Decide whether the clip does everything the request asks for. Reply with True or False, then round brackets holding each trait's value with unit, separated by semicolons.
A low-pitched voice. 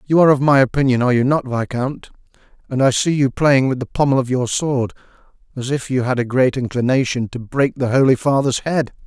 True (130 Hz)